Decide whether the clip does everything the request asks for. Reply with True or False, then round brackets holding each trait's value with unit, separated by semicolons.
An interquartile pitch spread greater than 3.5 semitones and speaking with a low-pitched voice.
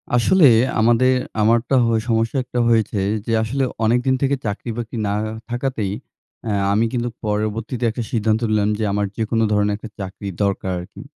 False (2.4 semitones; 115 Hz)